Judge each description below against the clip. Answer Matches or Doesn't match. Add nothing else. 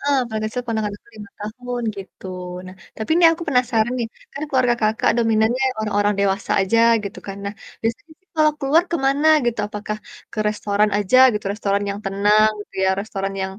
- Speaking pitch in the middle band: Doesn't match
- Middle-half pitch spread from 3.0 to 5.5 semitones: Matches